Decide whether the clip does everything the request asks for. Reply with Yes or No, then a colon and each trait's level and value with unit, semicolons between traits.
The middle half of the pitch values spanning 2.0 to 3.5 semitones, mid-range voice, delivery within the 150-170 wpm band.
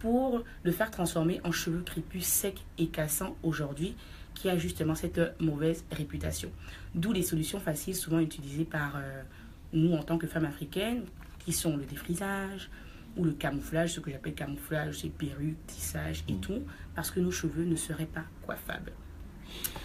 Yes: average, 3.1 semitones; medium, 160 Hz; average, 165 wpm